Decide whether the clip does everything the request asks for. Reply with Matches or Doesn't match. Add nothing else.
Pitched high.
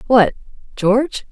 Matches